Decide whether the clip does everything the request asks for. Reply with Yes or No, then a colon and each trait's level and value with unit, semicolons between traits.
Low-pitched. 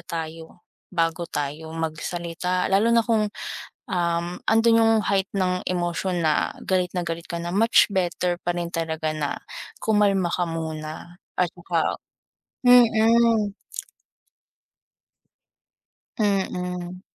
No: medium, 175 Hz